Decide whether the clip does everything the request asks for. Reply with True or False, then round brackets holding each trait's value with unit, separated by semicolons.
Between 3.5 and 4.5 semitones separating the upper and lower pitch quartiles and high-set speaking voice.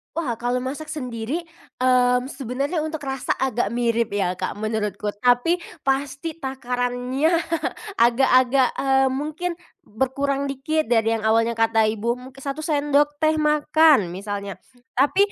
True (3.9 semitones; 260 Hz)